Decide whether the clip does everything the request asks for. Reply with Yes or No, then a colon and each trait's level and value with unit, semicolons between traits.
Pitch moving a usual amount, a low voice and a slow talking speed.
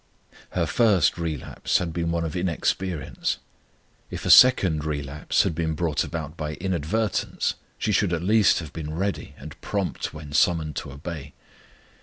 No: average, 3.3 semitones; very low, 85 Hz; average, 155 wpm